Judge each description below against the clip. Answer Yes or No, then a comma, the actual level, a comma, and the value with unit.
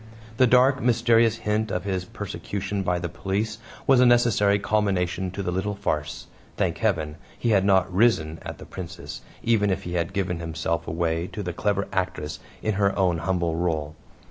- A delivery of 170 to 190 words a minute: Yes, average, 180 wpm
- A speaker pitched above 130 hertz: No, very low, 95 Hz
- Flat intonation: No, average, 3.5 semitones